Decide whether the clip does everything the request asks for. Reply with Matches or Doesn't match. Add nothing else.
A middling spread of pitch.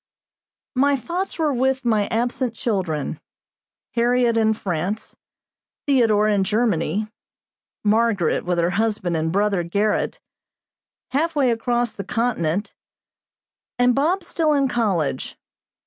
Matches